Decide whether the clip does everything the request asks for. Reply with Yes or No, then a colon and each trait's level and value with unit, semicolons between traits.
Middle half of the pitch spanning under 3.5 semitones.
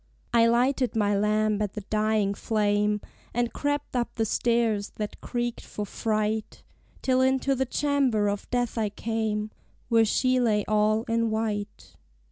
Yes: narrow, 2.4 semitones